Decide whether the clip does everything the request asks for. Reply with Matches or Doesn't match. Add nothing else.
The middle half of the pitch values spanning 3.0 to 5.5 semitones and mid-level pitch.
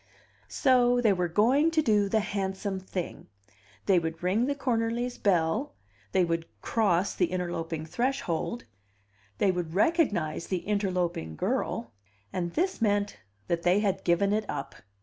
Doesn't match